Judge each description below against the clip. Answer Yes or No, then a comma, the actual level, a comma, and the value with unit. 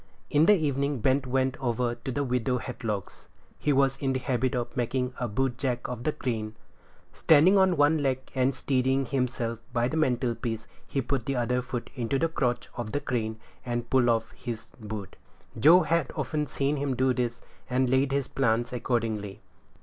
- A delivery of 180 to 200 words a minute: Yes, average, 185 wpm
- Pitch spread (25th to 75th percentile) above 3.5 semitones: No, narrow, 2.4 semitones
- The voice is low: Yes, low, 130 Hz